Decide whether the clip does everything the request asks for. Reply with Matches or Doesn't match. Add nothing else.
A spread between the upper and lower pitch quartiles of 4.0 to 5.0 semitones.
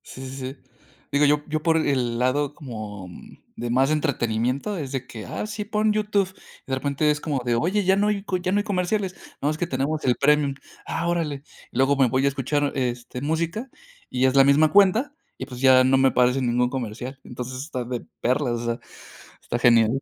Matches